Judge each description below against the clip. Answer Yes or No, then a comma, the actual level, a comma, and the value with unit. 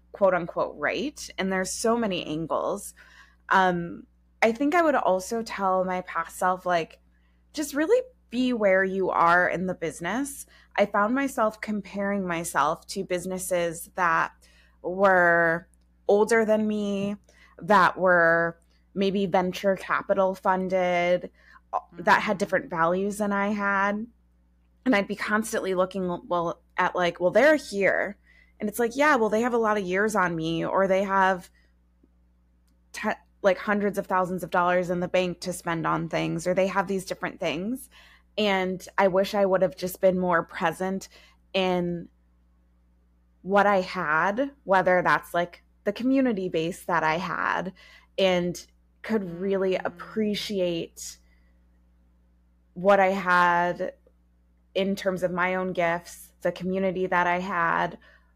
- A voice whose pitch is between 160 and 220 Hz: Yes, medium, 185 Hz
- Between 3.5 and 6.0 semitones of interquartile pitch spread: No, average, 2.9 semitones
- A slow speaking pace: No, average, 145 wpm